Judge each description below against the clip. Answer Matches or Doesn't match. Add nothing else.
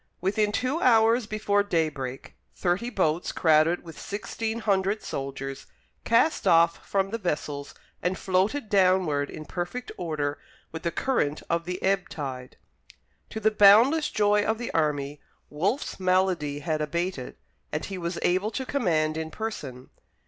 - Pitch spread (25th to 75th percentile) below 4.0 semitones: Doesn't match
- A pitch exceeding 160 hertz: Matches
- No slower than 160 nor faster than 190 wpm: Doesn't match